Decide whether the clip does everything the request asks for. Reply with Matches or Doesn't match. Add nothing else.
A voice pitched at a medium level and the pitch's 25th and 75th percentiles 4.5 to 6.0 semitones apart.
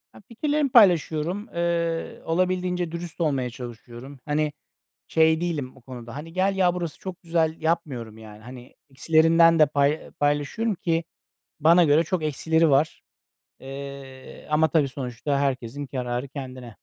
Doesn't match